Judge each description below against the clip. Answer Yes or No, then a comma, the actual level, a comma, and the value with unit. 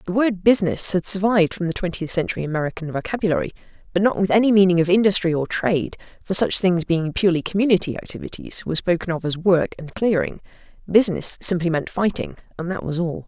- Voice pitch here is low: No, medium, 180 Hz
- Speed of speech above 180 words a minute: Yes, average, 190 wpm